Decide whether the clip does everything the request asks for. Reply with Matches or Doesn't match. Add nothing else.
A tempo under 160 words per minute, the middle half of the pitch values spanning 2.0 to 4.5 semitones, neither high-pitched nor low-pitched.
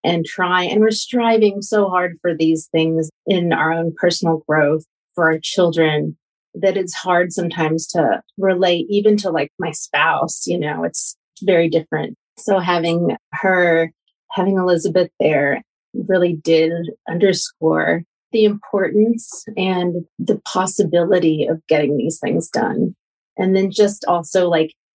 Matches